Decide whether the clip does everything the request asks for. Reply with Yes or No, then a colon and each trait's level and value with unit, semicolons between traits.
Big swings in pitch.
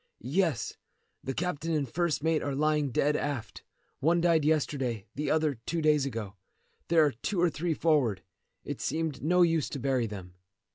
No: average, 3.6 semitones